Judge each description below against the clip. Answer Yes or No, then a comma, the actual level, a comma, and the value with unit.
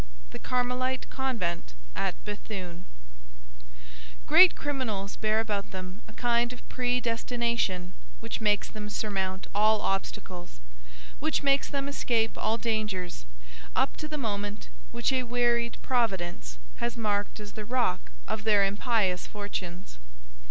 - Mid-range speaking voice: No, high, 215 Hz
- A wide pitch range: No, average, 3.8 semitones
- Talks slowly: Yes, slow, 125 wpm